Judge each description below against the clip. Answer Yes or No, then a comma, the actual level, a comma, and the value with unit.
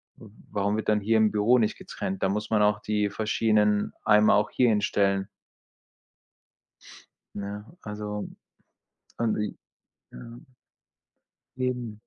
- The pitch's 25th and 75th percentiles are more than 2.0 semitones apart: No, narrow, 1.0 semitones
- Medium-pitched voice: No, low, 105 Hz